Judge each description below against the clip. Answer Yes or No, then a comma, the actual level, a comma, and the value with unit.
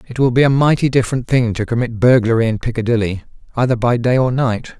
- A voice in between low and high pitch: No, low, 120 Hz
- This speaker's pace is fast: Yes, fast, 215 wpm